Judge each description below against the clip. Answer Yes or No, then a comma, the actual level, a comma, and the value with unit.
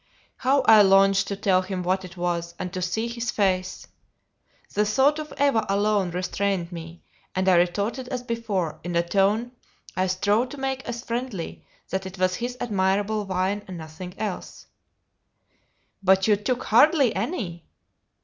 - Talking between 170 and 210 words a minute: No, average, 160 wpm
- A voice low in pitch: No, high, 195 Hz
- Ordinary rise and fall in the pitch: Yes, average, 4.1 semitones